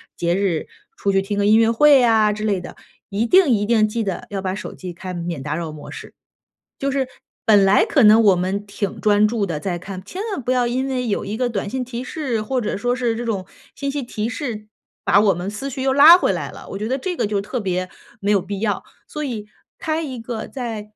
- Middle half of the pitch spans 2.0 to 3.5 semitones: No, average, 4.1 semitones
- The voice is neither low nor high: No, high, 215 Hz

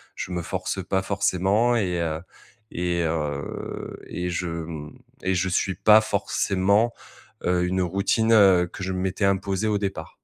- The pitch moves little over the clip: Yes, narrow, 2.1 semitones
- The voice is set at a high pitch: No, very low, 95 Hz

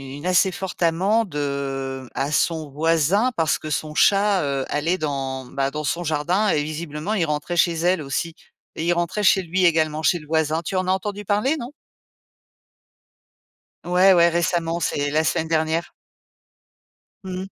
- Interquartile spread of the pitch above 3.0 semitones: Yes, average, 3.5 semitones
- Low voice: No, medium, 165 Hz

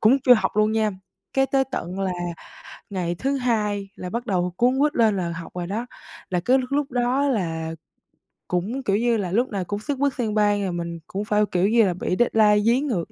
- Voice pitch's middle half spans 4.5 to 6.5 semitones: Yes, average, 5.1 semitones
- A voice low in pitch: No, high, 210 Hz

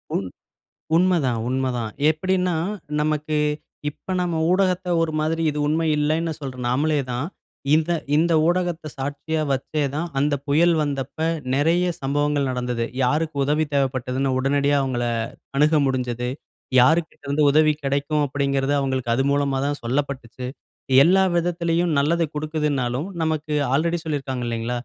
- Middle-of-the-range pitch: Yes, medium, 145 Hz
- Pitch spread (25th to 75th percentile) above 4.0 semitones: No, average, 3.3 semitones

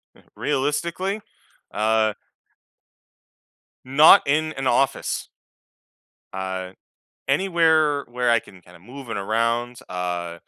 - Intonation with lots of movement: Yes, wide, 7.1 semitones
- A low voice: Yes, low, 120 Hz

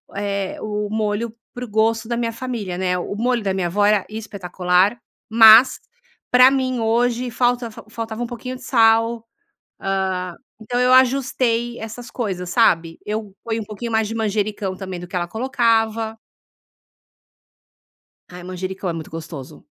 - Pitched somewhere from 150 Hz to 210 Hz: No, high, 220 Hz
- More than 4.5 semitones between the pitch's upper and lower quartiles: No, average, 3.6 semitones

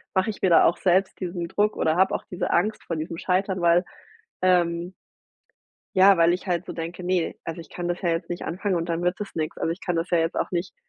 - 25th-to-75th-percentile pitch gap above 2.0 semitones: No, narrow, 1.7 semitones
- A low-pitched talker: No, medium, 175 Hz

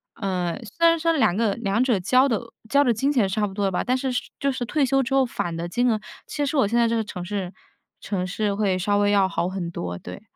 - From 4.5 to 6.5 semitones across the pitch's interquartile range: Yes, average, 5.2 semitones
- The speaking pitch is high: Yes, high, 215 Hz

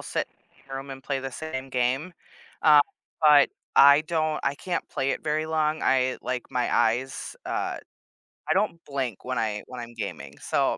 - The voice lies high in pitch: No, low, 135 Hz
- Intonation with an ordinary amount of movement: Yes, average, 3.4 semitones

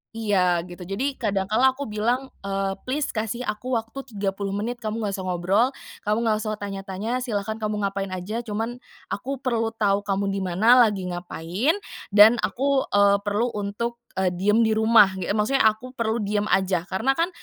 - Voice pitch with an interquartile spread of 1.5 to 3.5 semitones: Yes, average, 3.2 semitones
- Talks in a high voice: Yes, high, 215 Hz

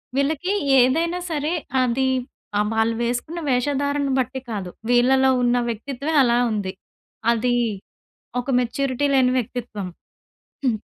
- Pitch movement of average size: Yes, average, 3.0 semitones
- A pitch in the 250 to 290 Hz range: Yes, very high, 255 Hz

